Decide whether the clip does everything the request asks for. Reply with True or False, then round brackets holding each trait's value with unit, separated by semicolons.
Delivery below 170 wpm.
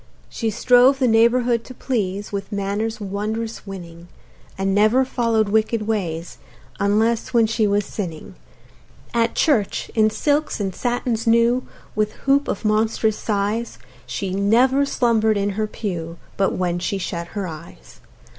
True (145 wpm)